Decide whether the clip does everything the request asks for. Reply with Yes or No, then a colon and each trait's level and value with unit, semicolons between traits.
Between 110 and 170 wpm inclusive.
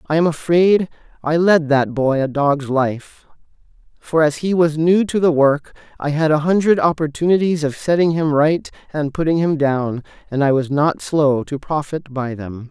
No: average, 190 wpm